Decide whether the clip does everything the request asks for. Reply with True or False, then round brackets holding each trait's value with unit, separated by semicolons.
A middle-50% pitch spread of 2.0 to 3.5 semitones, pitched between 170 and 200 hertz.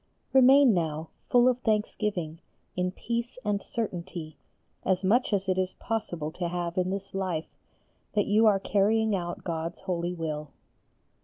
False (3.9 semitones; 190 Hz)